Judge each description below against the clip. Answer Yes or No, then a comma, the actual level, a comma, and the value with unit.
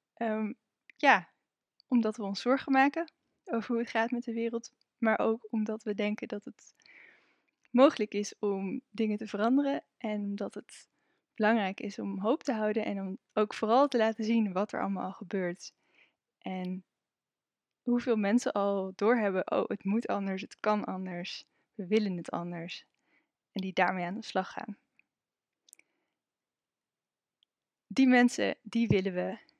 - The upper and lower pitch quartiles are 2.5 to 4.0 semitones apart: Yes, average, 2.8 semitones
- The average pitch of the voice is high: Yes, high, 215 Hz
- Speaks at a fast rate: No, average, 155 wpm